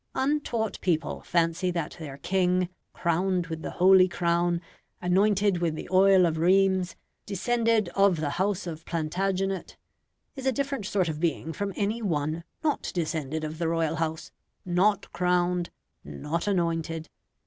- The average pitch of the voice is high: No, medium, 180 Hz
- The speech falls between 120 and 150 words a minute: Yes, average, 145 wpm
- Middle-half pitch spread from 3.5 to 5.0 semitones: No, average, 3.0 semitones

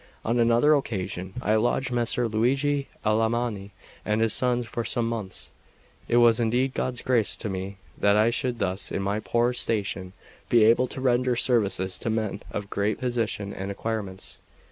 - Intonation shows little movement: No, average, 3.0 semitones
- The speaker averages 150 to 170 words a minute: Yes, average, 165 wpm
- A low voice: Yes, low, 115 Hz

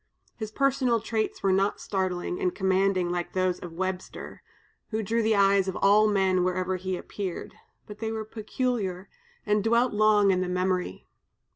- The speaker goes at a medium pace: Yes, average, 165 wpm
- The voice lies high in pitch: Yes, high, 195 Hz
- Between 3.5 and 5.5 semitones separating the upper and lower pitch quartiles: No, average, 2.8 semitones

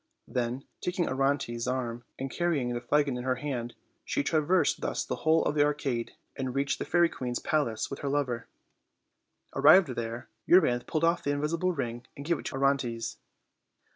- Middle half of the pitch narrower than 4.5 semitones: Yes, average, 3.8 semitones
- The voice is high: No, low, 135 Hz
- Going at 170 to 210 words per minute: Yes, average, 175 wpm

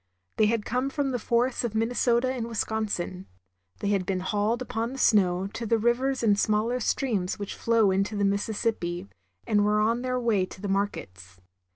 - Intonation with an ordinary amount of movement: Yes, average, 3.1 semitones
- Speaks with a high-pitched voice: Yes, high, 220 Hz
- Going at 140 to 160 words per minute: No, average, 190 wpm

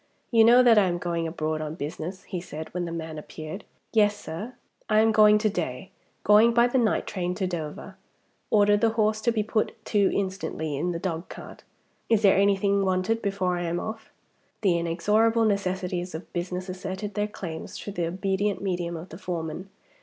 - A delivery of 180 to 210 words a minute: Yes, average, 190 wpm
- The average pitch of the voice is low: No, high, 190 Hz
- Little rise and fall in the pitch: No, average, 3.5 semitones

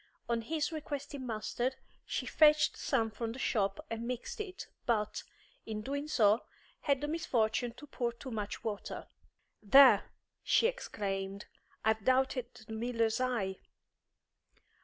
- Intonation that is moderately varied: Yes, average, 4.3 semitones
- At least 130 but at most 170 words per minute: Yes, slow, 135 wpm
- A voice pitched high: Yes, high, 240 Hz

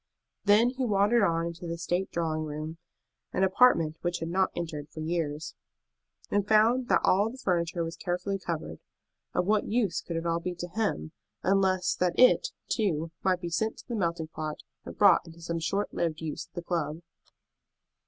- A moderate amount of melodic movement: Yes, average, 3.4 semitones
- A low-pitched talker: No, medium, 175 Hz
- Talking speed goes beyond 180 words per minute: Yes, average, 190 wpm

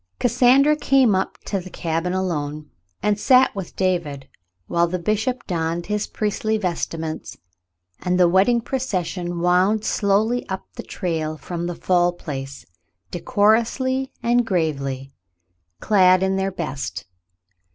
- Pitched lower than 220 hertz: Yes, medium, 185 Hz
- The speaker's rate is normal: No, slow, 130 wpm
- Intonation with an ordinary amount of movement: Yes, average, 4.3 semitones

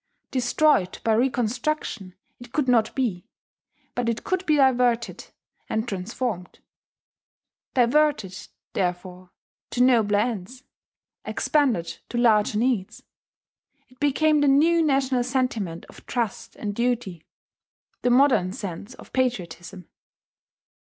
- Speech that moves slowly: Yes, slow, 110 wpm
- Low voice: No, high, 240 Hz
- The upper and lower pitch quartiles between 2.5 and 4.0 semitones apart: No, average, 4.7 semitones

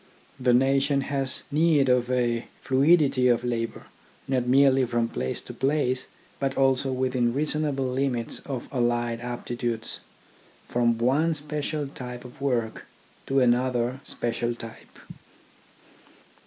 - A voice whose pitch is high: No, low, 130 Hz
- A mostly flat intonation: Yes, narrow, 2.3 semitones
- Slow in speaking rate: Yes, slow, 120 wpm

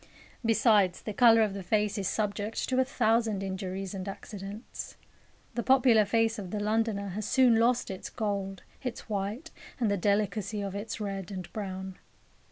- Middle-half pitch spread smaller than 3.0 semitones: Yes, narrow, 2.5 semitones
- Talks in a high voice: Yes, high, 210 Hz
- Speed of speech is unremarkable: Yes, average, 170 wpm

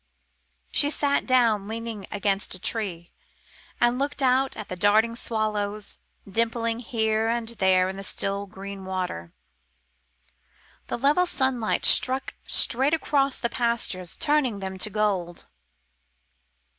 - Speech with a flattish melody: No, average, 4.0 semitones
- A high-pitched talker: Yes, high, 220 Hz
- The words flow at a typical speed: No, slow, 120 wpm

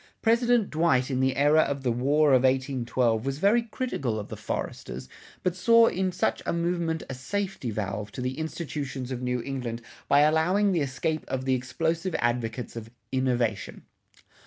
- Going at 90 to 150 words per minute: No, average, 170 wpm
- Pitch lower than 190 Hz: Yes, low, 135 Hz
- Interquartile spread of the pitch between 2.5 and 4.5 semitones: No, average, 5.2 semitones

